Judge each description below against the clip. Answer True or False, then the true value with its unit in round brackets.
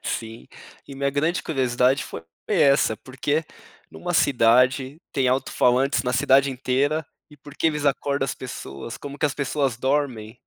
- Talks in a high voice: False (135 Hz)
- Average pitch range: False (2.3 semitones)